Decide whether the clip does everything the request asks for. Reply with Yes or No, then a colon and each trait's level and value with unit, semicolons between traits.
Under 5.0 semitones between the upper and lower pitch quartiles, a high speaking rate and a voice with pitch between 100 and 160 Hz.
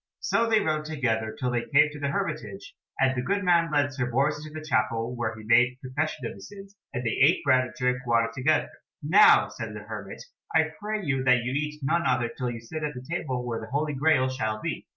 Yes: average, 4.0 semitones; fast, 235 wpm; low, 135 Hz